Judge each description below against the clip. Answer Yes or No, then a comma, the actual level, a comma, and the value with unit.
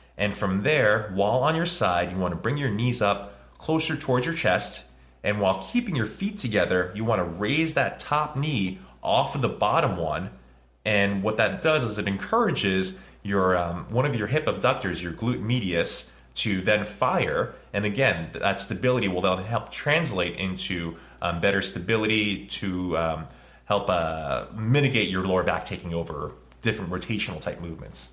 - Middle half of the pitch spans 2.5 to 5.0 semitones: No, wide, 5.5 semitones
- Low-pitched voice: Yes, low, 100 Hz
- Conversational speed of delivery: Yes, average, 175 wpm